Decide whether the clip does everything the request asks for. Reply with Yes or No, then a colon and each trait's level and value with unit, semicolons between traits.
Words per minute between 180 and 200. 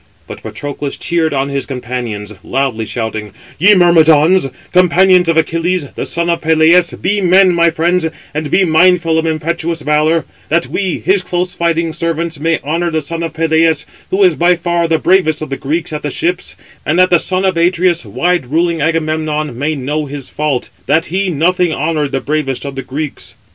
Yes: average, 185 wpm